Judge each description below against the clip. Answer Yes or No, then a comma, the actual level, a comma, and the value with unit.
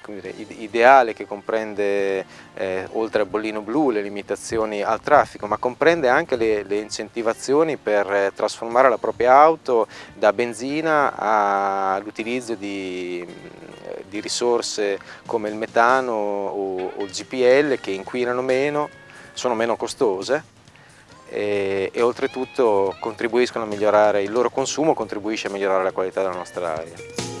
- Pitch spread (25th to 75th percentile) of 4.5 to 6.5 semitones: No, average, 3.7 semitones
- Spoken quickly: No, average, 135 wpm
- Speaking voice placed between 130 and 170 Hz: No, low, 110 Hz